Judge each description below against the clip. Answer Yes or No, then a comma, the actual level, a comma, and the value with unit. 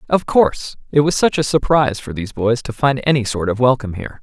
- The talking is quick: Yes, fast, 240 wpm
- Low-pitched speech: Yes, low, 130 Hz